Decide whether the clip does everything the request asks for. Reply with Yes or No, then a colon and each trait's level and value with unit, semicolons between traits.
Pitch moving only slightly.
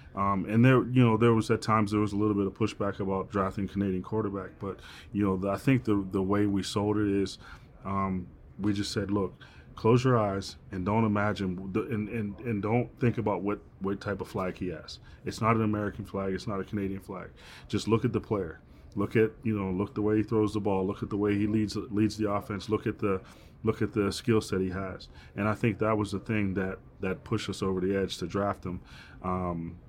Yes: narrow, 2.0 semitones